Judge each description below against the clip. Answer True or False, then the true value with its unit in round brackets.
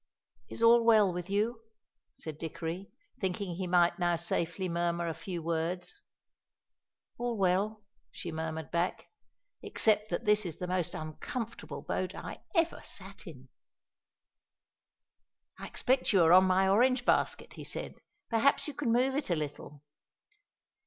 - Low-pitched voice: False (185 Hz)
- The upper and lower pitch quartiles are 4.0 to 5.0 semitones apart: True (4.7 semitones)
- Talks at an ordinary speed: True (145 wpm)